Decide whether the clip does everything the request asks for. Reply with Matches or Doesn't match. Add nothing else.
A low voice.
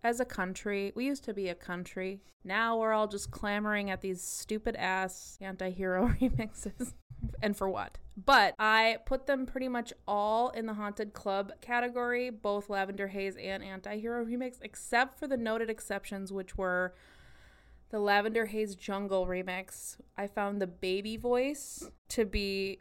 Doesn't match